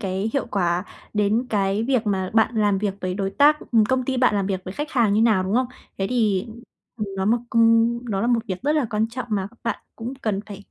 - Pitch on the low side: No, high, 215 Hz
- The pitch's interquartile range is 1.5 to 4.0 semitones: Yes, average, 3.4 semitones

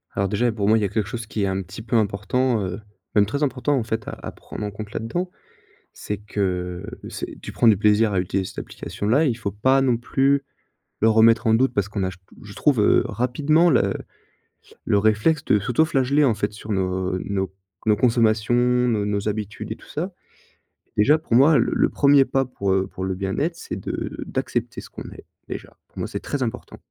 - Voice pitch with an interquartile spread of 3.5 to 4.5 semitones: Yes, average, 4.2 semitones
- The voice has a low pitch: Yes, low, 110 Hz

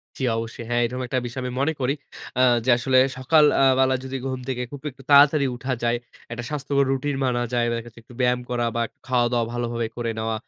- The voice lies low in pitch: Yes, low, 125 Hz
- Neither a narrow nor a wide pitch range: No, narrow, 2.0 semitones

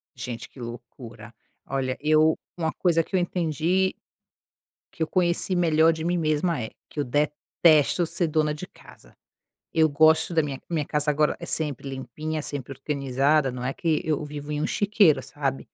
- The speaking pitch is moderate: Yes, medium, 150 Hz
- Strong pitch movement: No, average, 2.9 semitones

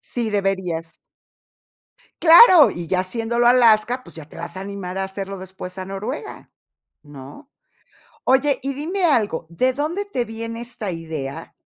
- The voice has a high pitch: Yes, high, 215 Hz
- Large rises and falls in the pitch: Yes, wide, 5.7 semitones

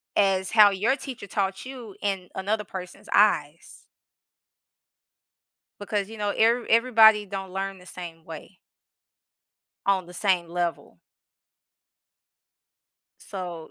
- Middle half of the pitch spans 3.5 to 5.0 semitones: No, average, 2.8 semitones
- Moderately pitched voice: No, high, 195 Hz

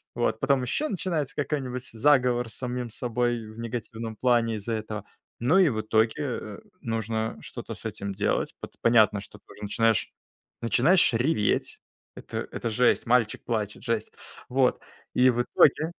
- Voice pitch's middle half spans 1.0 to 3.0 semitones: Yes, narrow, 2.6 semitones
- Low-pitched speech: Yes, low, 120 Hz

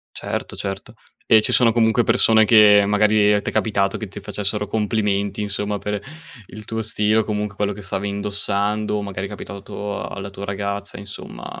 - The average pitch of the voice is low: Yes, low, 105 Hz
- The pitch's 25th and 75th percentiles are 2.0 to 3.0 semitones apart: No, narrow, 1.1 semitones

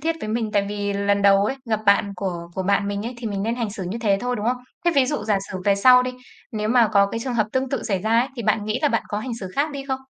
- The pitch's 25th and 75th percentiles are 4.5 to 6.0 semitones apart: No, average, 3.7 semitones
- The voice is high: Yes, high, 215 Hz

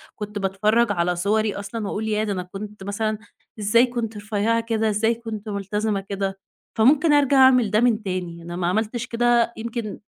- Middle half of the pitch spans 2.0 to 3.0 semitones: Yes, narrow, 2.5 semitones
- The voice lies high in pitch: Yes, high, 215 Hz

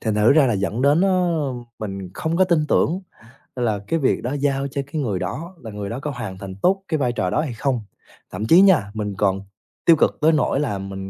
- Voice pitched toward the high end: No, low, 130 Hz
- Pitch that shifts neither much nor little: No, wide, 7.1 semitones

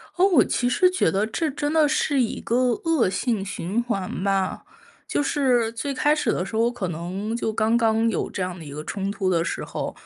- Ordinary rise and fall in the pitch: No, wide, 5.9 semitones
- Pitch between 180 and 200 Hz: No, high, 225 Hz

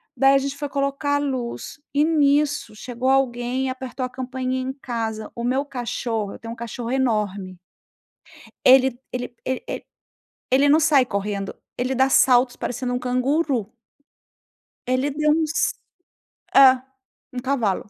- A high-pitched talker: Yes, very high, 255 Hz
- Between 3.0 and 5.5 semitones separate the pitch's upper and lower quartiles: No, narrow, 2.4 semitones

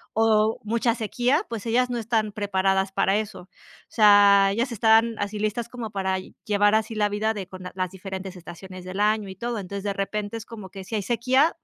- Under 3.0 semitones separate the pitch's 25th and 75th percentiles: Yes, narrow, 2.6 semitones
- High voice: Yes, high, 210 Hz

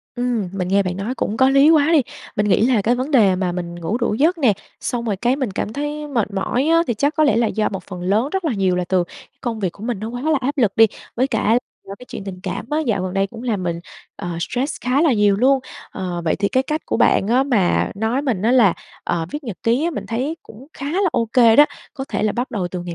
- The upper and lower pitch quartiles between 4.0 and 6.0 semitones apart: Yes, wide, 5.5 semitones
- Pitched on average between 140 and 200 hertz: No, high, 230 Hz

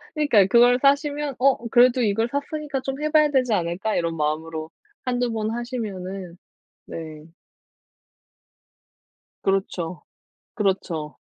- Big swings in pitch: Yes, wide, 6.9 semitones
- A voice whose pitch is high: Yes, high, 225 Hz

